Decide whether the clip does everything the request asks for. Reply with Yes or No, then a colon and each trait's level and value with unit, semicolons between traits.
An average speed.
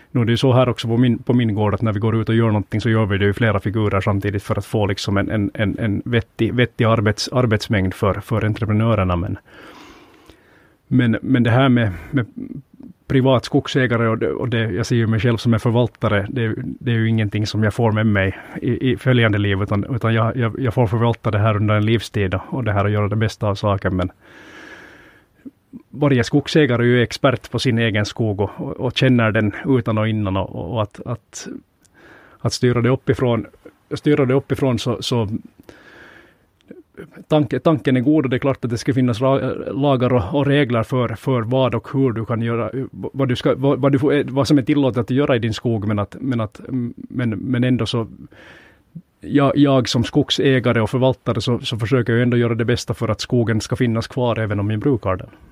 No: fast, 215 wpm